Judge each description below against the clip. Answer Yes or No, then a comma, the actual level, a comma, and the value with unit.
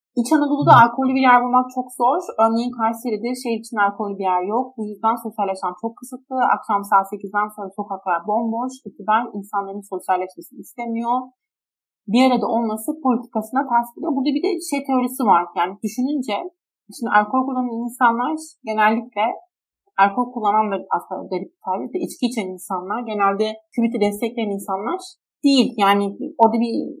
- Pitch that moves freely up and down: No, average, 3.6 semitones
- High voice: Yes, high, 230 Hz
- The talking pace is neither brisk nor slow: No, fast, 150 wpm